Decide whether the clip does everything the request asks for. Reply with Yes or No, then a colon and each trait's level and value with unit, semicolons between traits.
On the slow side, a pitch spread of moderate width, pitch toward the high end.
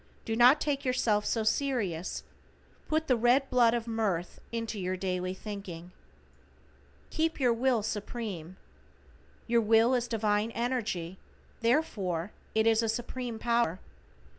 Yes: slow, 130 wpm; average, 3.5 semitones; high, 225 Hz